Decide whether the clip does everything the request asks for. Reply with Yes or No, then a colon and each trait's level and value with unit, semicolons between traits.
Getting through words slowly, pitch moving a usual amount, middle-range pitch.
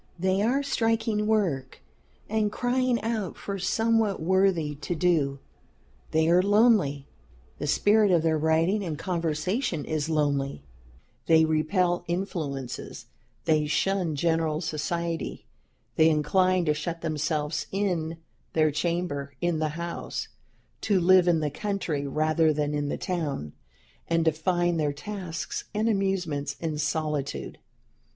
Yes: slow, 130 wpm; average, 4.0 semitones; medium, 165 Hz